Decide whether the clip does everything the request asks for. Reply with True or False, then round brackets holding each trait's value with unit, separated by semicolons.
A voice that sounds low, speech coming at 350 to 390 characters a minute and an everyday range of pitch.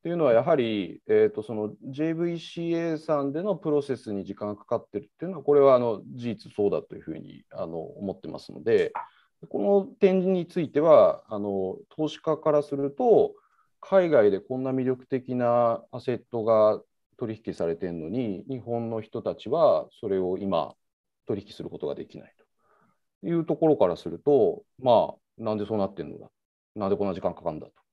False (130 Hz; 355 characters per minute; 7.7 semitones)